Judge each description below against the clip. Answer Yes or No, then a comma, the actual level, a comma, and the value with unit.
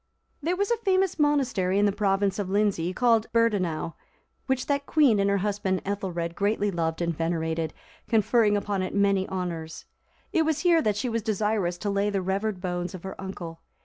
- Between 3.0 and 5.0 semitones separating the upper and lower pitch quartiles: Yes, average, 3.9 semitones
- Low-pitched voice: No, high, 200 Hz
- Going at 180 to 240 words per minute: Yes, average, 185 wpm